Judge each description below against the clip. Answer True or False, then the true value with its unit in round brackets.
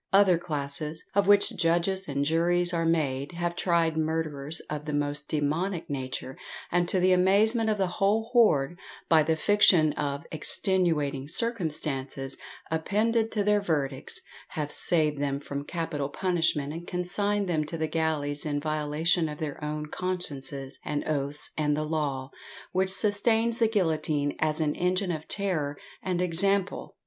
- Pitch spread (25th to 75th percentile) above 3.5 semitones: True (4.0 semitones)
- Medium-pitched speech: True (160 Hz)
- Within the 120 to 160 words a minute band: True (155 wpm)